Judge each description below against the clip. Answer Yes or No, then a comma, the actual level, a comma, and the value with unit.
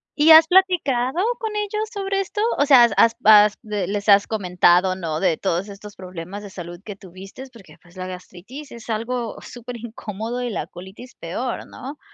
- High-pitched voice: Yes, high, 215 Hz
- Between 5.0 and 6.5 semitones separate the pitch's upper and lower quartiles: Yes, wide, 5.5 semitones